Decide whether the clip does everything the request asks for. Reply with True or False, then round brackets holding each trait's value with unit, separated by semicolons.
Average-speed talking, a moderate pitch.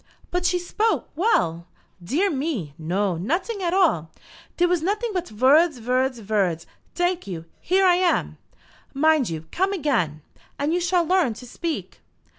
False (155 wpm; 310 Hz)